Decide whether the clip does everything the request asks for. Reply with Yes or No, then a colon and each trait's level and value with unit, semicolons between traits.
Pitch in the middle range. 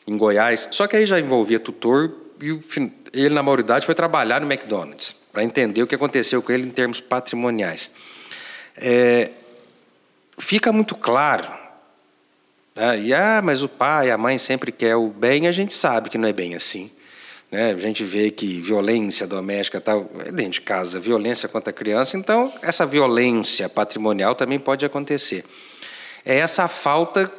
No: low, 125 Hz